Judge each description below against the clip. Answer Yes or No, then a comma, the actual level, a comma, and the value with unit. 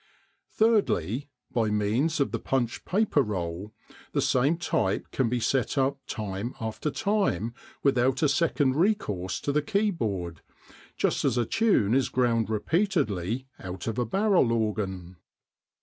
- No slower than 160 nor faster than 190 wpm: No, average, 140 wpm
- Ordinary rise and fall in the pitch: No, wide, 6.2 semitones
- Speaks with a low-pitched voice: Yes, low, 125 Hz